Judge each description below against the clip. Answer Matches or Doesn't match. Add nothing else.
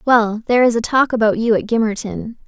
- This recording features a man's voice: Doesn't match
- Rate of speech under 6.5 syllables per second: Matches